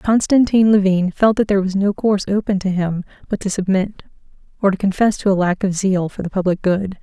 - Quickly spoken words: Yes, fast, 220 wpm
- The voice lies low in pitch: No, high, 195 Hz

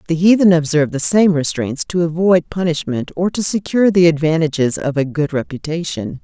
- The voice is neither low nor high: Yes, medium, 165 Hz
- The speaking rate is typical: Yes, average, 175 wpm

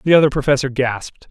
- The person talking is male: Yes, male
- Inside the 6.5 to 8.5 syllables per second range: Yes, 6.8 syllables/s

